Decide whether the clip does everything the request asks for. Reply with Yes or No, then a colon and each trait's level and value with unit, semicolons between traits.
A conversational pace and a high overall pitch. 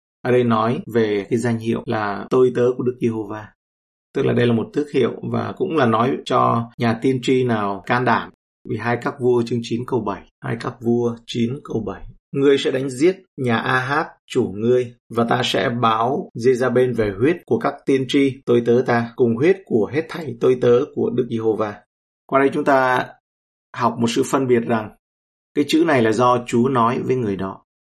No: average, 215 wpm; low, 120 Hz